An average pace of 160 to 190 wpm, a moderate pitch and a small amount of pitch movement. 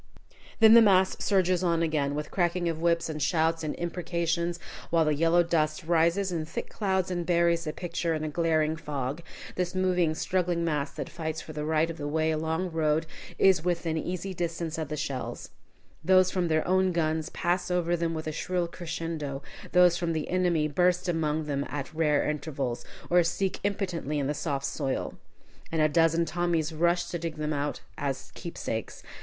Yes: average, 185 wpm; medium, 165 Hz; narrow, 2.2 semitones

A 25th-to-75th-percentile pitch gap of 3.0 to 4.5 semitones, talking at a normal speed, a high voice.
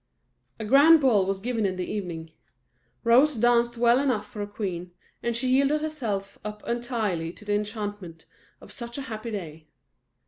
Yes: average, 3.5 semitones; average, 170 wpm; high, 215 Hz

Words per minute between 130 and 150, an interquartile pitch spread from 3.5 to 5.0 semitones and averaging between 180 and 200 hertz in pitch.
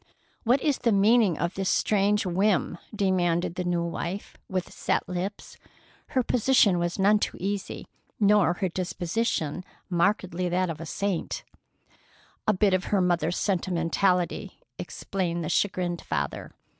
No: average, 140 wpm; average, 2.8 semitones; medium, 185 Hz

